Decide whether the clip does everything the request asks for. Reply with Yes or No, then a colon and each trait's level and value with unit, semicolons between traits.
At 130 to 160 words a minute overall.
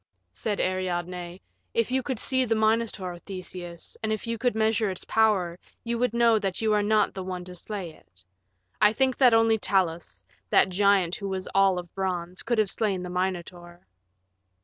No: average, 185 wpm